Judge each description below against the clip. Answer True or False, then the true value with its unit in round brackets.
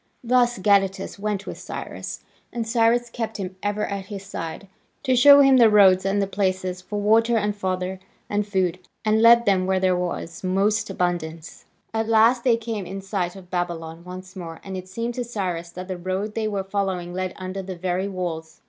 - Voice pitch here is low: False (195 Hz)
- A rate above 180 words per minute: True (195 wpm)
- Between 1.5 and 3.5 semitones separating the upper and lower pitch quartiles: True (2.9 semitones)